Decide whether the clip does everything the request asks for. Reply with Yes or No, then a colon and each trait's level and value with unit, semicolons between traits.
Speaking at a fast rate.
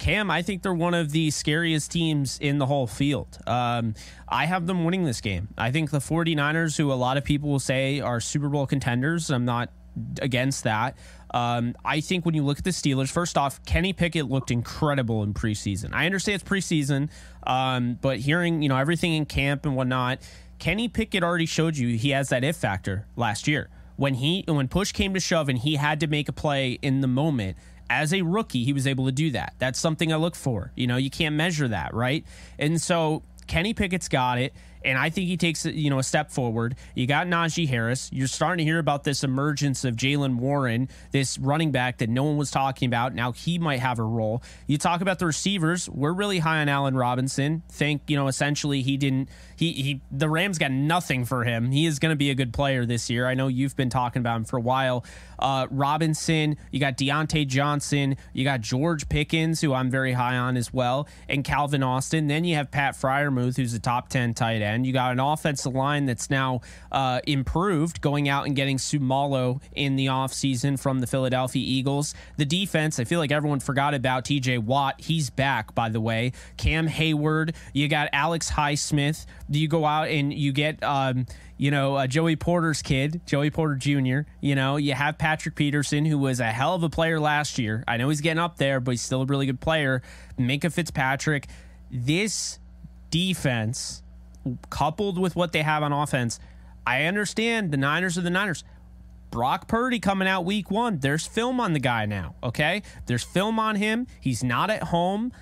Yes: fast, 210 wpm